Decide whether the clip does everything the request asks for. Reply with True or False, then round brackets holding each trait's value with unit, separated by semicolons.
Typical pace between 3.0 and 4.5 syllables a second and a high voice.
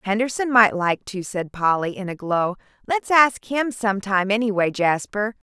False (4.9 syllables/s; 210 Hz)